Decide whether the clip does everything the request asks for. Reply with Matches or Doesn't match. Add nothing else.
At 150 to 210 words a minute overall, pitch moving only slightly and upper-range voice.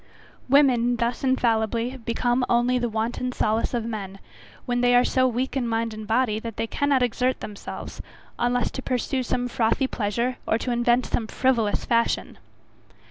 Matches